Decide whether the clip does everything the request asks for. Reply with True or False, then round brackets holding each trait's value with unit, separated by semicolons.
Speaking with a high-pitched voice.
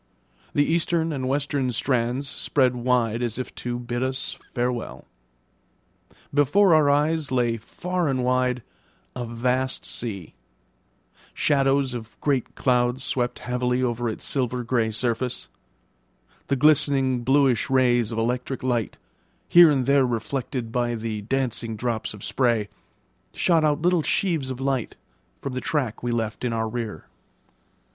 False (125 Hz)